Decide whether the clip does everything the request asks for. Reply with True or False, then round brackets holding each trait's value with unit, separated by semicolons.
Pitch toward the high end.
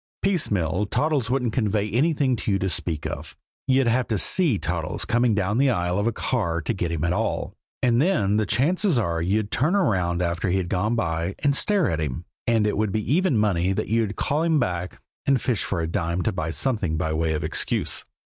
False (105 Hz)